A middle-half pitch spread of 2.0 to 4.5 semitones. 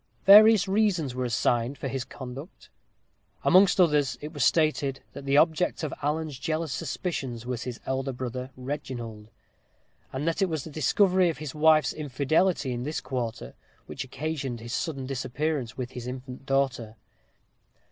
Yes: average, 3.9 semitones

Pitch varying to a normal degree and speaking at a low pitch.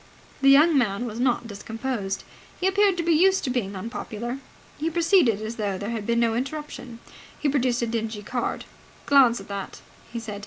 No: average, 4.5 semitones; high, 240 Hz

